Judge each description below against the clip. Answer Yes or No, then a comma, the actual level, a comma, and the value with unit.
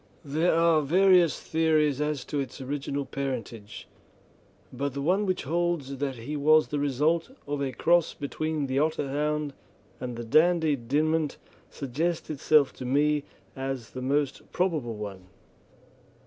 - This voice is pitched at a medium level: Yes, medium, 145 Hz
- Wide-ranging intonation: No, average, 2.9 semitones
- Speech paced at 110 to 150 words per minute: Yes, average, 140 wpm